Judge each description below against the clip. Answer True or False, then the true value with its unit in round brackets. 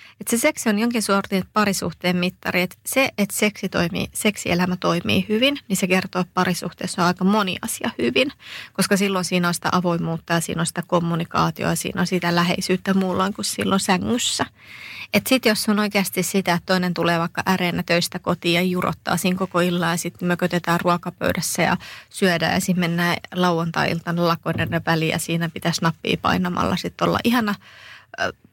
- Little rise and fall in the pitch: True (2.2 semitones)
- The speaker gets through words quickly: True (175 wpm)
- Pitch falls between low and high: True (180 Hz)